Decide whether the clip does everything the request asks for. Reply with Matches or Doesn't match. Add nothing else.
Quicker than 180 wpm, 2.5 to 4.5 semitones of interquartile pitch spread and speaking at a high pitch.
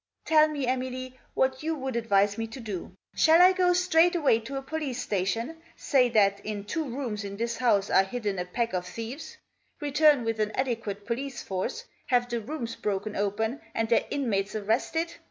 Doesn't match